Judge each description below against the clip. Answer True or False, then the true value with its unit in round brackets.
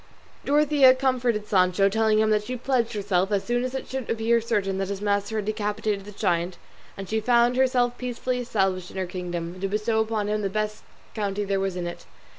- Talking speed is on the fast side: True (210 wpm)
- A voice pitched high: True (210 Hz)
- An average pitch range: True (3.5 semitones)